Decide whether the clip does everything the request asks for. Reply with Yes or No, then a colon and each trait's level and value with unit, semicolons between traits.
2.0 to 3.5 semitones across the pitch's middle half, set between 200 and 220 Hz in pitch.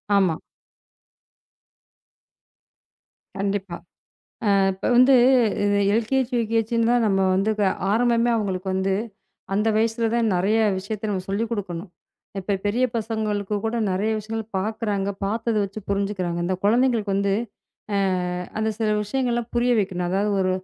Yes: average, 2.7 semitones; high, 210 Hz